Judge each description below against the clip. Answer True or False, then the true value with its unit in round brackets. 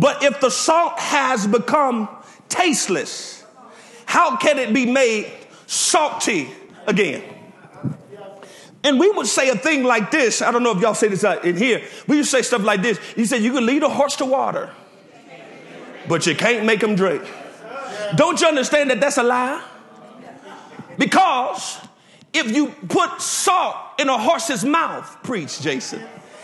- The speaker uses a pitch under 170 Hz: False (255 Hz)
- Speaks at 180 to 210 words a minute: False (160 wpm)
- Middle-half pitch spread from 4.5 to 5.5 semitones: True (4.9 semitones)